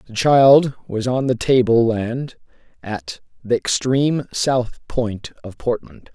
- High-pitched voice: No, low, 120 Hz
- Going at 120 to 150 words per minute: Yes, slow, 135 wpm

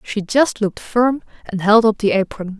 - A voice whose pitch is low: No, high, 215 Hz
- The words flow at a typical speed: No, fast, 210 wpm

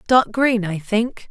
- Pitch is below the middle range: No, high, 220 Hz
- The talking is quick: No, average, 185 wpm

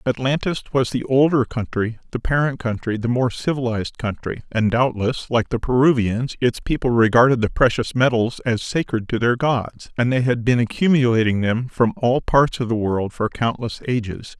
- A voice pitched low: Yes, low, 120 Hz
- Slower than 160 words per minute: No, average, 180 wpm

